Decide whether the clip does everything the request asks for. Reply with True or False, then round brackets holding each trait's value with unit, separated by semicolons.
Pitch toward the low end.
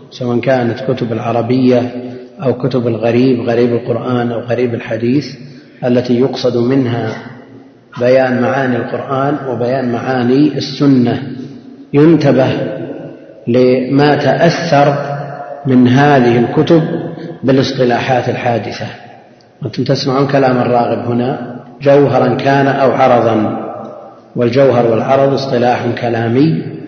True (125 Hz)